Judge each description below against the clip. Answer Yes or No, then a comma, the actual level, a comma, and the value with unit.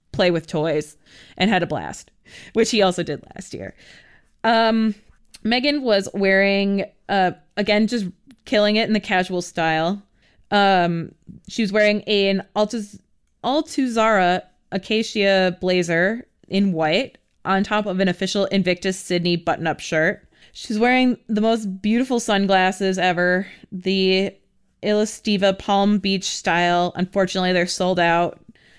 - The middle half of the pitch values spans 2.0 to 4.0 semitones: Yes, average, 2.8 semitones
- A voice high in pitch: Yes, high, 195 Hz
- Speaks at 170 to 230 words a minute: No, slow, 135 wpm